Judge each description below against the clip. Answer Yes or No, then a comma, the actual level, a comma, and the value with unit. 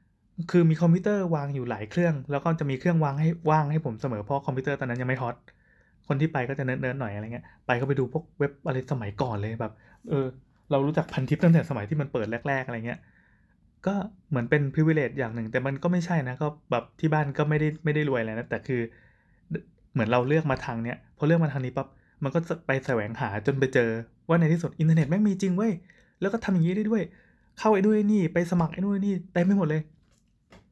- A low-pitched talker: No, medium, 145 Hz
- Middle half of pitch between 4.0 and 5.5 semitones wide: Yes, average, 4.9 semitones